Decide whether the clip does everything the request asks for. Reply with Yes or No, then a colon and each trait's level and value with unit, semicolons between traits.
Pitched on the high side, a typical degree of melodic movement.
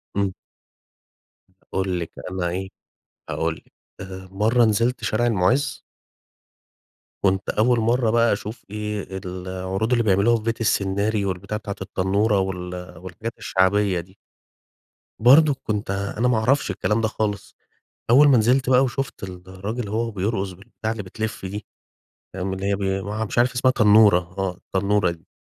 No: low, 105 Hz; average, 3.2 semitones